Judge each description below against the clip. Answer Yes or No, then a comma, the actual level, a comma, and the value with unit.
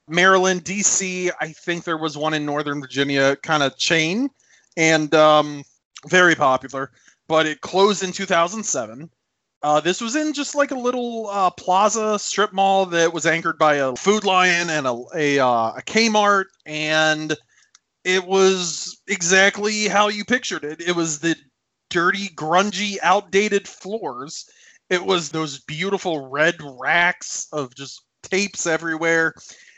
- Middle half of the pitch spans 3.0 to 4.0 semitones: No, average, 4.4 semitones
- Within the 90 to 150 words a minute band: Yes, average, 145 wpm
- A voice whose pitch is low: No, medium, 175 Hz